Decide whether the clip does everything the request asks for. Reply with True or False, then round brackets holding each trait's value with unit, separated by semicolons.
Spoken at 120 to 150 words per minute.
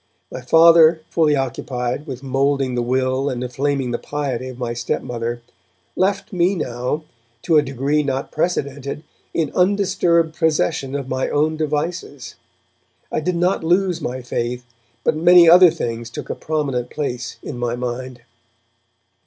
True (145 wpm)